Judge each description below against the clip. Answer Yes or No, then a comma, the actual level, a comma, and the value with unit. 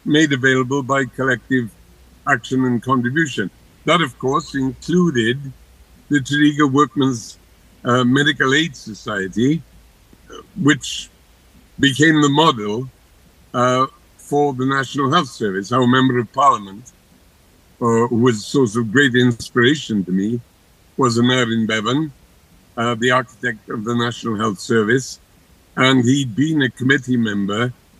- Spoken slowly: Yes, slow, 125 wpm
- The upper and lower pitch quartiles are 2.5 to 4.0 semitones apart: No, average, 5.3 semitones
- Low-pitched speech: Yes, low, 125 Hz